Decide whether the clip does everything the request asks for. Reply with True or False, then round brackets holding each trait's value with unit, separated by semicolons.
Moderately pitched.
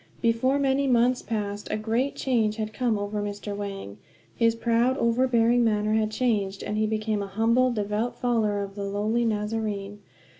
False (220 Hz)